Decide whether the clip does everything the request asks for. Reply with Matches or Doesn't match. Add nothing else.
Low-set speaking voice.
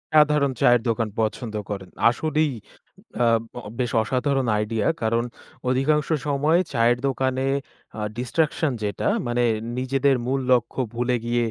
Matches